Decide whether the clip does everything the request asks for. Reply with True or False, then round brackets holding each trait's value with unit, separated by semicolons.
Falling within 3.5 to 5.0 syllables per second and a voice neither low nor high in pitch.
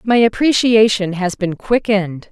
False (4.5 syllables/s; 210 Hz)